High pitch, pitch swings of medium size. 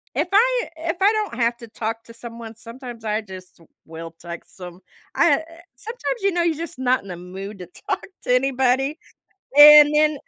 No: high, 245 Hz; wide, 6.4 semitones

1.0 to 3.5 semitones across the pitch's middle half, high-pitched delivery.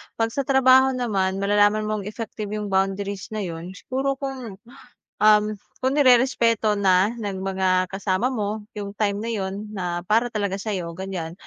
Yes: average, 3.0 semitones; high, 205 Hz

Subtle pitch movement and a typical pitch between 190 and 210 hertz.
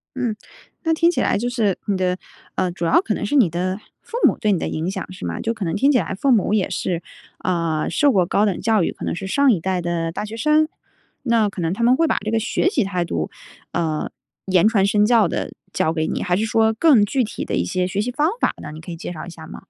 No: average, 5.0 semitones; high, 200 Hz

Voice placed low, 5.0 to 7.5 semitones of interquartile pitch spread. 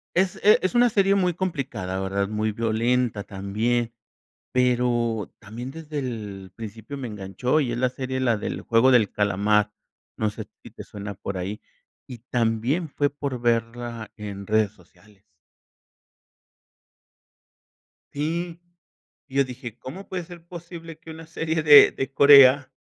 Yes: low, 120 Hz; wide, 5.5 semitones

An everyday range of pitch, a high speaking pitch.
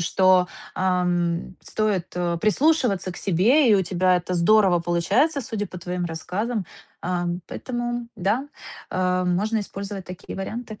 Yes: average, 3.8 semitones; high, 195 Hz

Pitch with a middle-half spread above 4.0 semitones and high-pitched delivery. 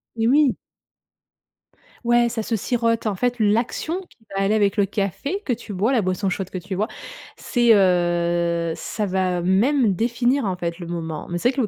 Yes: average, 4.7 semitones; high, 205 Hz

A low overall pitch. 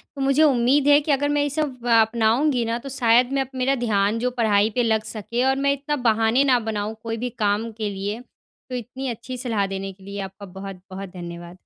No: high, 230 Hz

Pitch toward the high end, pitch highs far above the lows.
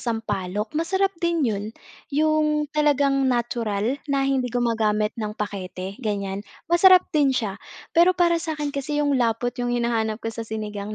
Yes: high, 245 Hz; wide, 6.0 semitones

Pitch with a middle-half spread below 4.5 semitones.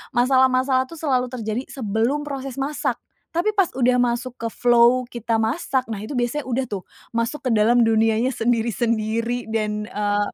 Yes: average, 2.7 semitones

